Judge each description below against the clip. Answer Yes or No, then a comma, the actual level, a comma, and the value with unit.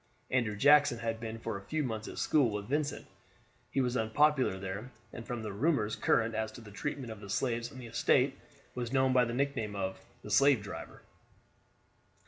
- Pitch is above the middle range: No, low, 115 Hz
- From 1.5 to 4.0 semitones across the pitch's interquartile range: Yes, average, 3.6 semitones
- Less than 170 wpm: No, average, 195 wpm